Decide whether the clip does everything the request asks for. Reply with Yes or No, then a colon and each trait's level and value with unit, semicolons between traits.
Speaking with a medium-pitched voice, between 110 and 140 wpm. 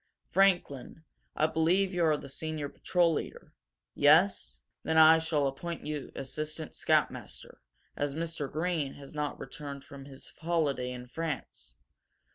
Yes: medium, 155 Hz; slow, 135 wpm